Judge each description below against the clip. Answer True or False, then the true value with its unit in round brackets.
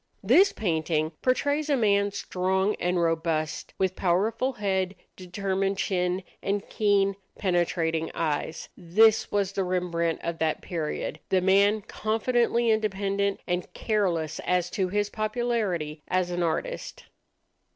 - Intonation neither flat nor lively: True (3.4 semitones)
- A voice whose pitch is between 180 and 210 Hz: True (190 Hz)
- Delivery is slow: True (125 wpm)